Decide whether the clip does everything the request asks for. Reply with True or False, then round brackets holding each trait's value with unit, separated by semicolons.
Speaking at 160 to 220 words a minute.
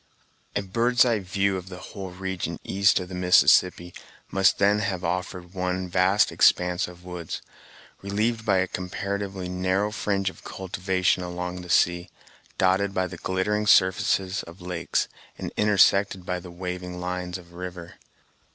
False (150 wpm)